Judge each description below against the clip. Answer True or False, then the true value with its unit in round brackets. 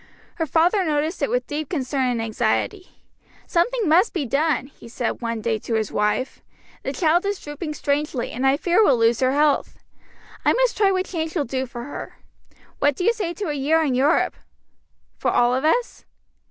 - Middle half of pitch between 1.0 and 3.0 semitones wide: False (5.3 semitones)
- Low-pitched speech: False (295 Hz)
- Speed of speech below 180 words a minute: False (195 wpm)